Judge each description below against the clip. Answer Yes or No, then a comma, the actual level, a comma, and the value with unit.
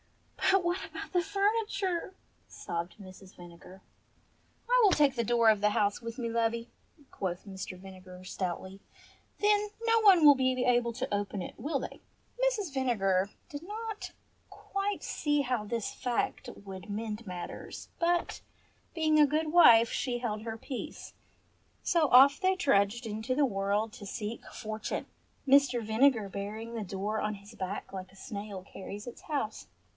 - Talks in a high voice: Yes, high, 230 Hz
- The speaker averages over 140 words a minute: Yes, average, 160 wpm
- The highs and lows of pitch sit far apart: Yes, wide, 6.7 semitones